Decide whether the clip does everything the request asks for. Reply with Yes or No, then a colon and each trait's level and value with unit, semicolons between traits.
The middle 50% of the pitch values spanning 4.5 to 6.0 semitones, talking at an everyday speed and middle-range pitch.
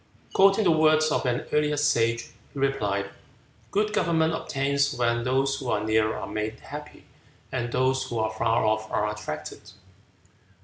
No: average, 5.3 semitones; average, 160 wpm; low, 130 Hz